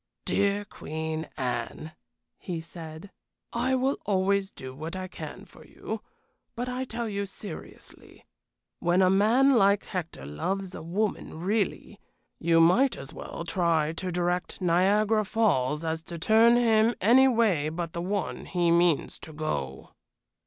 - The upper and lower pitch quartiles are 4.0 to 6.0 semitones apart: Yes, average, 4.8 semitones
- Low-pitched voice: No, medium, 185 Hz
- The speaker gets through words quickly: No, average, 145 wpm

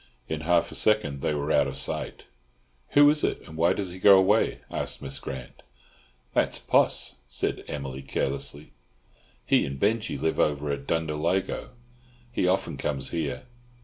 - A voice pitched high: No, very low, 75 Hz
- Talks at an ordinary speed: Yes, average, 160 wpm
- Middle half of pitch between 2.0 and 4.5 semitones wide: No, average, 5.1 semitones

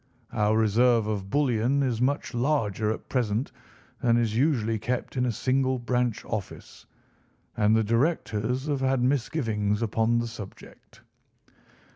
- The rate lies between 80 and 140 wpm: Yes, slow, 135 wpm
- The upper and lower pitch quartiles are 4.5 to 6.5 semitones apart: No, average, 3.0 semitones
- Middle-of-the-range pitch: No, low, 120 Hz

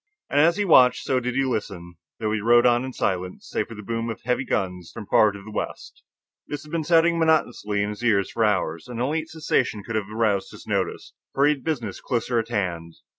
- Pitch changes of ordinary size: Yes, average, 4.6 semitones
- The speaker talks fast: Yes, fast, 235 wpm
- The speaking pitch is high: No, low, 115 Hz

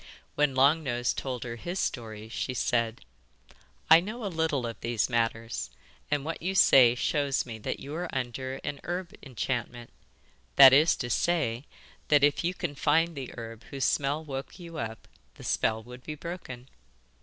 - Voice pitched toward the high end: No, low, 135 Hz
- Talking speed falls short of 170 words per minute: No, average, 175 wpm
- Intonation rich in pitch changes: No, average, 5.0 semitones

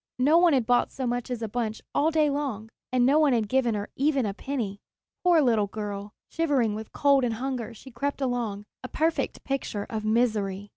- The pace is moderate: No, fast, 210 wpm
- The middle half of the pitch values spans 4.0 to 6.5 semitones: Yes, average, 4.3 semitones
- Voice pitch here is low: No, high, 245 Hz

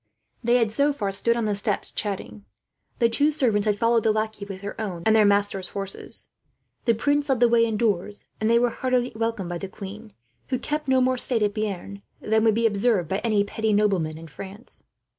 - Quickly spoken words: Yes, fast, 215 wpm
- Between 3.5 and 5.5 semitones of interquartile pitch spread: No, average, 2.7 semitones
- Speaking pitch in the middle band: No, high, 215 Hz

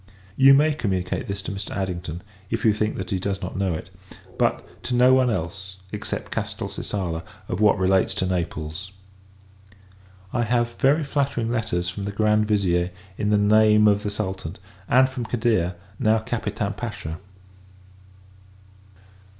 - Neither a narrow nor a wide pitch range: Yes, average, 3.5 semitones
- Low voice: Yes, low, 105 Hz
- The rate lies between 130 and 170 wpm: Yes, average, 150 wpm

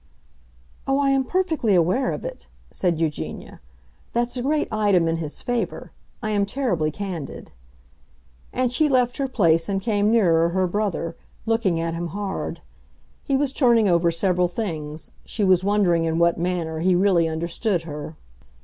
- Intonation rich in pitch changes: Yes, wide, 5.9 semitones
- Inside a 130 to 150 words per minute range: No, average, 160 wpm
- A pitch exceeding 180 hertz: Yes, high, 190 Hz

